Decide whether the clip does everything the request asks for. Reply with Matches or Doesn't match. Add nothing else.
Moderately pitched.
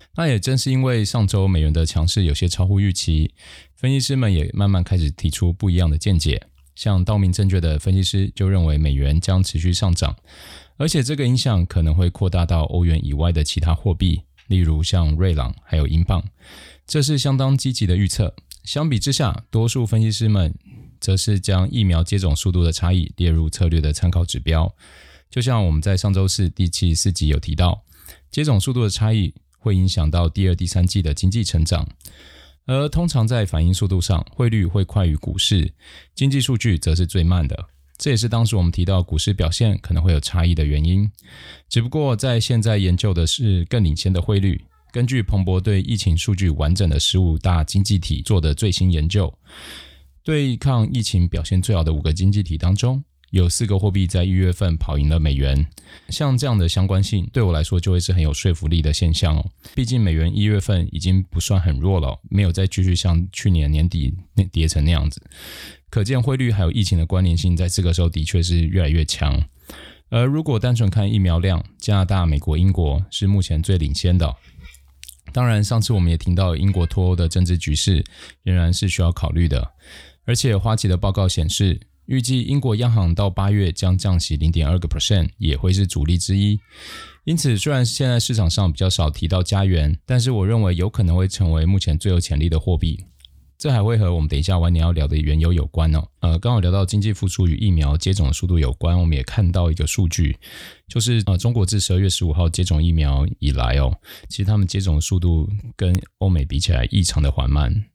Doesn't match